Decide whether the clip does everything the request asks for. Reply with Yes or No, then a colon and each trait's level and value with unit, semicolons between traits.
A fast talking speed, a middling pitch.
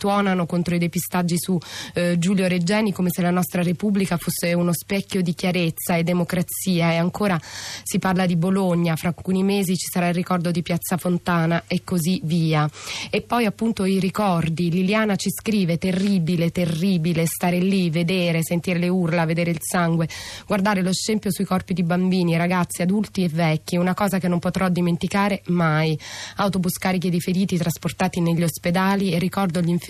Yes: fast, 175 wpm; medium, 180 Hz